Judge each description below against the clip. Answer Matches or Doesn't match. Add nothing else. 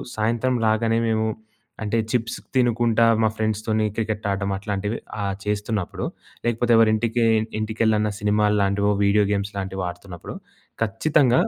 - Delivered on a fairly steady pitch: Matches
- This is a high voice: Doesn't match